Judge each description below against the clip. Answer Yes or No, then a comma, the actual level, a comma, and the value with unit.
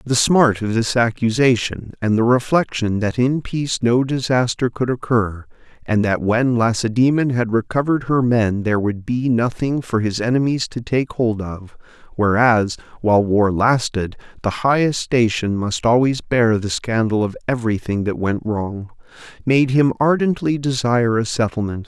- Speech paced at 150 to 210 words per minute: Yes, average, 155 wpm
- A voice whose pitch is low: Yes, low, 120 Hz